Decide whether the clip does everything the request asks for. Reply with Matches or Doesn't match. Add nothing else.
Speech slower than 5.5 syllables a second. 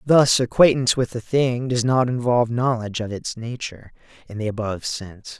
Doesn't match